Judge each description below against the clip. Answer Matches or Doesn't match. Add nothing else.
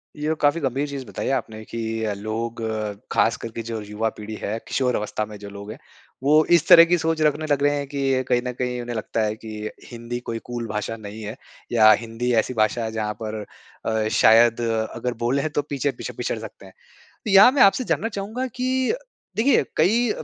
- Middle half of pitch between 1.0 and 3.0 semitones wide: Doesn't match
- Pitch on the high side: Doesn't match